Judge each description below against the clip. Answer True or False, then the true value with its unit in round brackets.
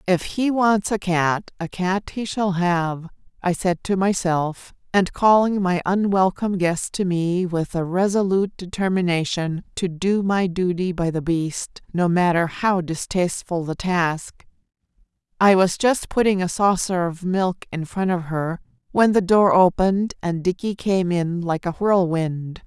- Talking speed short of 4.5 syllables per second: True (4.1 syllables/s)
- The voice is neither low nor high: True (180 Hz)